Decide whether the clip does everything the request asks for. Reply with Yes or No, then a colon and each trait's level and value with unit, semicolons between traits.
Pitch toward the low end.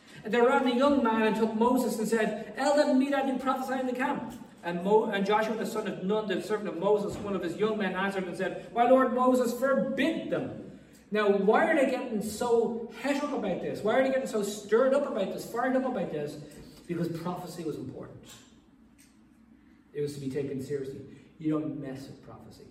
No: high, 220 Hz